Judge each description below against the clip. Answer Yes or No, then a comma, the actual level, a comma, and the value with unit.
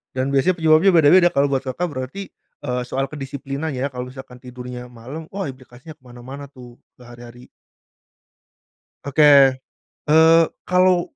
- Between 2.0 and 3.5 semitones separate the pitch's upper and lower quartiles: No, average, 4.1 semitones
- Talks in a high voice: No, low, 135 Hz